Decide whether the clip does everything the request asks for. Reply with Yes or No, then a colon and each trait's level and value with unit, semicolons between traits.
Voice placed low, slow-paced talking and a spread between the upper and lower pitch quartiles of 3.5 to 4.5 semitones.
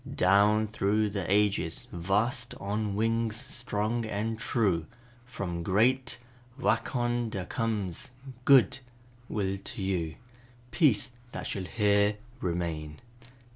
No: low, 105 Hz; slow, 110 wpm; average, 3.1 semitones